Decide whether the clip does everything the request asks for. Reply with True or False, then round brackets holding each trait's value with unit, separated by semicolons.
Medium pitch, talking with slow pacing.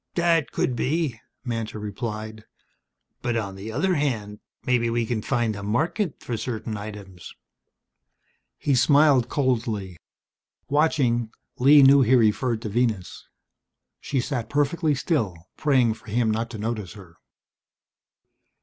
False (120 Hz; 130 wpm)